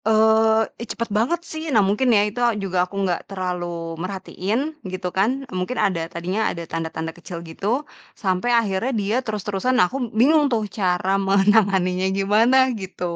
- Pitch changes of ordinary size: Yes, average, 3.3 semitones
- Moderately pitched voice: No, high, 200 Hz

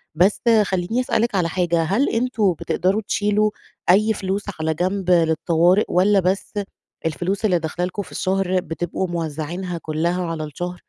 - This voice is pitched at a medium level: Yes, medium, 180 Hz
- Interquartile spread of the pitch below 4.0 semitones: Yes, average, 2.9 semitones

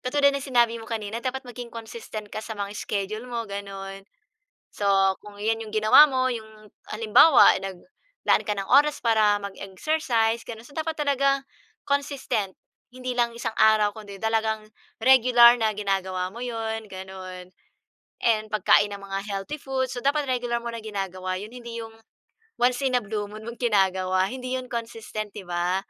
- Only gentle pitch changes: No, average, 3.5 semitones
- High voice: Yes, high, 225 Hz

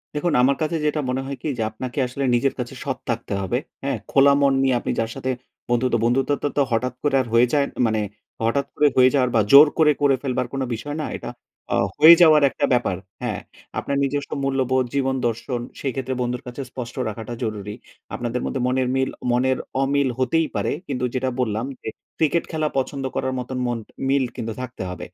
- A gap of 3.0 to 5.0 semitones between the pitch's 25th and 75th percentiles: No, narrow, 2.4 semitones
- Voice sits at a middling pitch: No, low, 130 Hz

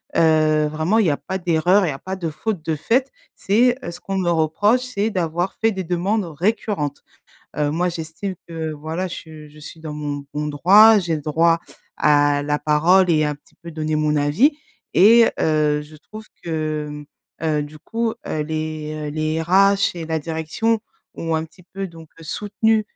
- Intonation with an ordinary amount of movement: Yes, average, 3.9 semitones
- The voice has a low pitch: No, medium, 160 Hz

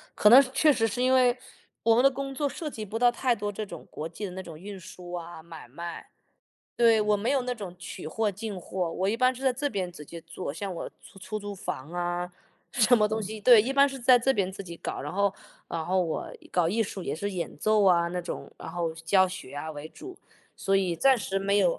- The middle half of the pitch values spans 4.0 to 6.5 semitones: Yes, average, 5.1 semitones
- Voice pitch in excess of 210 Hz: No, high, 200 Hz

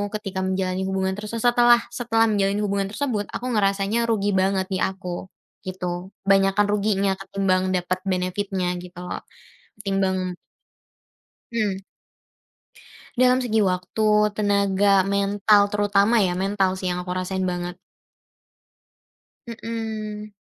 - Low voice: No, high, 195 Hz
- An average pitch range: No, narrow, 2.0 semitones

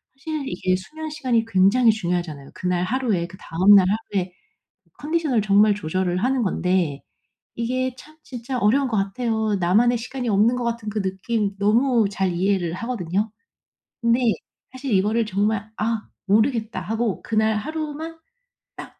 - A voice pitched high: Yes, high, 220 Hz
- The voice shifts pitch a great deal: No, average, 4.4 semitones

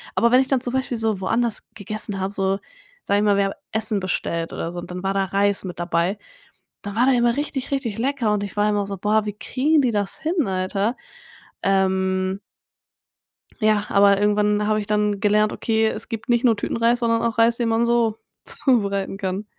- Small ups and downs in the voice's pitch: No, average, 3.0 semitones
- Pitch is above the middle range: Yes, high, 210 Hz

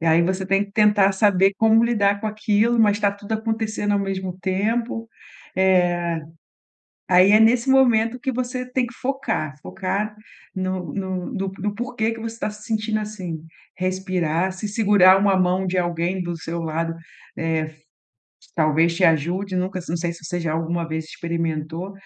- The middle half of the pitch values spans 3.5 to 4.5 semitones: Yes, average, 3.9 semitones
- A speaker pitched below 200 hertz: Yes, high, 190 Hz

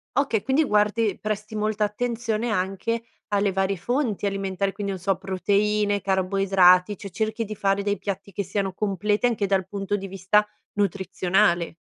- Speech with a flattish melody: Yes, narrow, 1.7 semitones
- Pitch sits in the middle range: No, high, 200 Hz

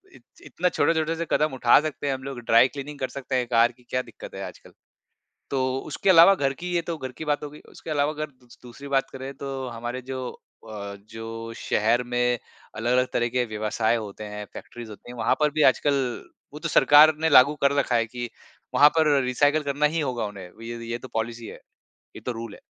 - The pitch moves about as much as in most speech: Yes, average, 3.8 semitones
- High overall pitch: No, low, 130 Hz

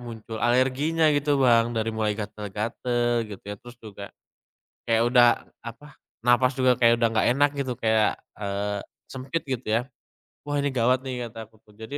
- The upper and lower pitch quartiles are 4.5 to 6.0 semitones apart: No, average, 2.7 semitones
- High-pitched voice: No, low, 120 Hz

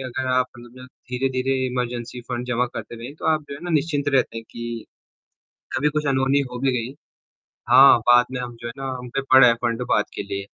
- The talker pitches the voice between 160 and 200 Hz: No, low, 125 Hz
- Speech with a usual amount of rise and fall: No, narrow, 2.0 semitones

